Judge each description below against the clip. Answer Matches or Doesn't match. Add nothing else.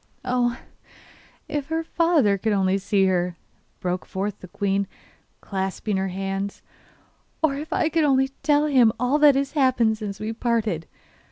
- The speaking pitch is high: Matches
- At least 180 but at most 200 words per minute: Doesn't match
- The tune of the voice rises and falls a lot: Matches